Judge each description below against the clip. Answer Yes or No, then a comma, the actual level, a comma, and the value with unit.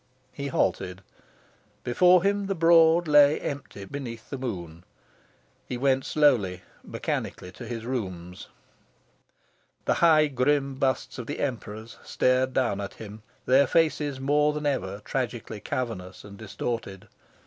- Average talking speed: No, slow, 130 wpm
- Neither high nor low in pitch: No, low, 130 Hz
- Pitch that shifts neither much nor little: No, wide, 5.9 semitones